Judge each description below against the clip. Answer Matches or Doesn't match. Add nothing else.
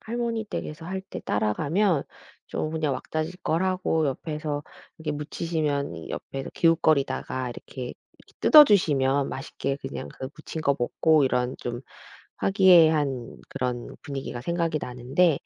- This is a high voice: Doesn't match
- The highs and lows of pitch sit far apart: Doesn't match